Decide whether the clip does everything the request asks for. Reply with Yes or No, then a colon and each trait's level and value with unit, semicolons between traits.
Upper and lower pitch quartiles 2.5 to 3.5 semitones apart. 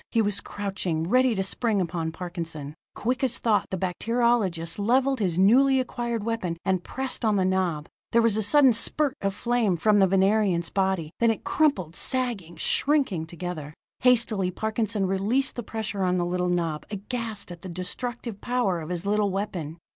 No: average, 4.8 semitones